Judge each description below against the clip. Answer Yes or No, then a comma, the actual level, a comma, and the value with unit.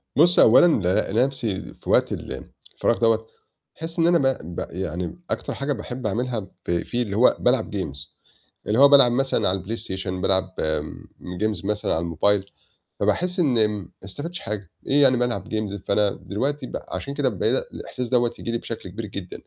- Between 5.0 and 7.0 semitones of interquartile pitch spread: Yes, average, 5.3 semitones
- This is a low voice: Yes, low, 110 Hz